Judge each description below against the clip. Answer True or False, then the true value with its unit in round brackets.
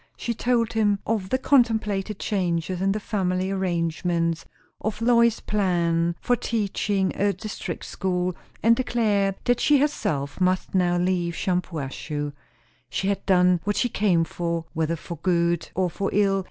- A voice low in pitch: False (190 Hz)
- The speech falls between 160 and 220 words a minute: False (150 wpm)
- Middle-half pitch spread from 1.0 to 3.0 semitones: False (3.7 semitones)